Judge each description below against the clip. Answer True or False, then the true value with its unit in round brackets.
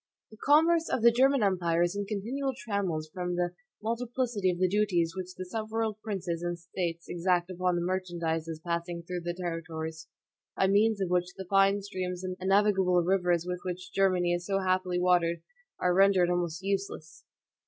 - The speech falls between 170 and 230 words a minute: True (175 wpm)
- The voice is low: False (185 Hz)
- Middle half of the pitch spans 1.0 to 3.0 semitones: True (2.5 semitones)